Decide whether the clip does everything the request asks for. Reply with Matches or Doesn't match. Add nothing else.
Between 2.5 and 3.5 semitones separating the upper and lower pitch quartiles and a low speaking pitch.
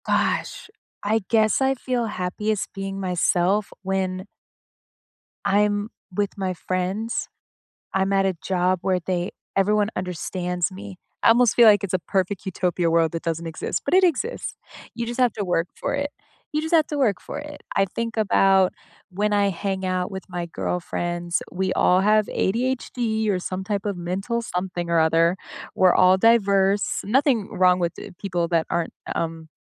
Doesn't match